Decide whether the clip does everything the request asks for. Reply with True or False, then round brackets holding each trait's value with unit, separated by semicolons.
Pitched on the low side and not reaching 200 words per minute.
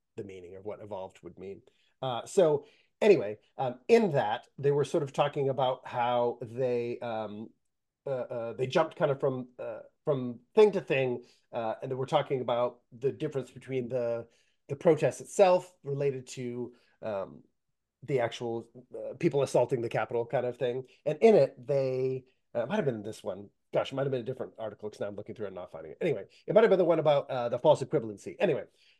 False (130 Hz; 205 wpm)